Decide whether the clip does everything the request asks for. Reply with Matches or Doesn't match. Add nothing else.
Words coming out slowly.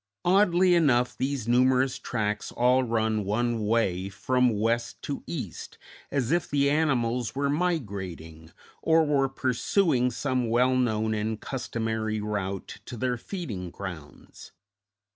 Matches